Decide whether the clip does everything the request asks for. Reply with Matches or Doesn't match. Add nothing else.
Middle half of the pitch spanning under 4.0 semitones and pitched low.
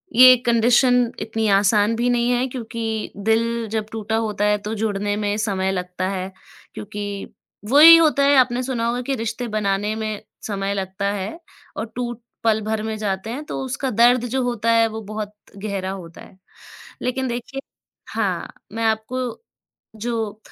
Doesn't match